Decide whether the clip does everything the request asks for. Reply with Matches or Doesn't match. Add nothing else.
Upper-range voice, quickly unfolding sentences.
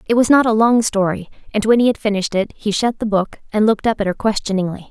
Matches